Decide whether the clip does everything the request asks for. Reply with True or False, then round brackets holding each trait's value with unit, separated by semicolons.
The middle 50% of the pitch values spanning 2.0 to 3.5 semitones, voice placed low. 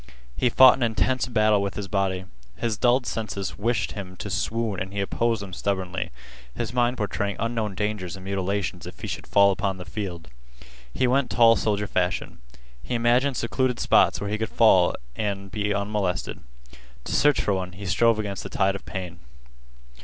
True (3.2 semitones; 100 Hz)